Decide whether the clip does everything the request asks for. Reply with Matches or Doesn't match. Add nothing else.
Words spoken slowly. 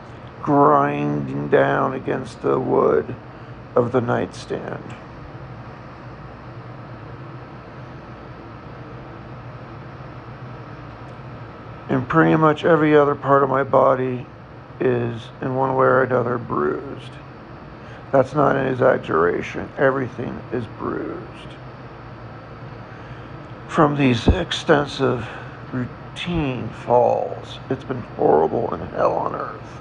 Matches